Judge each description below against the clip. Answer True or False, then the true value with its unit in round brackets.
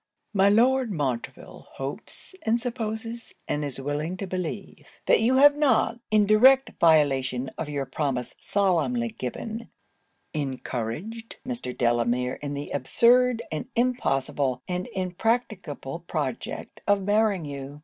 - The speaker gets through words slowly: True (125 wpm)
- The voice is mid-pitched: True (175 Hz)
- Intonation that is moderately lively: False (8.6 semitones)